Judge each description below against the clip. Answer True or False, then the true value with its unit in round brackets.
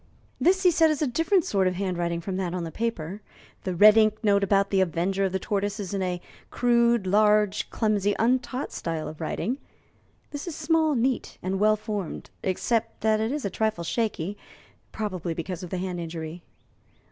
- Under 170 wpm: False (190 wpm)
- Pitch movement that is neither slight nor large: True (4.2 semitones)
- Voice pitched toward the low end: False (205 Hz)